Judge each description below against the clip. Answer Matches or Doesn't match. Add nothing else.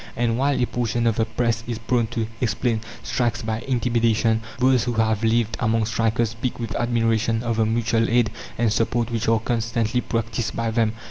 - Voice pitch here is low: Matches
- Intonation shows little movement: Matches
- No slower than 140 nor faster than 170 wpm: Doesn't match